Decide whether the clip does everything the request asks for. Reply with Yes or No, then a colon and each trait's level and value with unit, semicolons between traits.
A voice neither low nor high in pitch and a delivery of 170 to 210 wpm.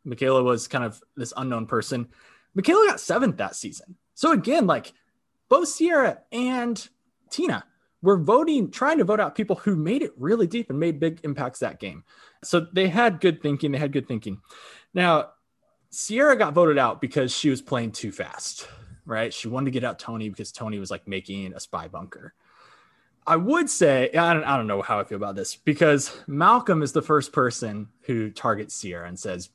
Yes: medium, 145 Hz; average, 195 wpm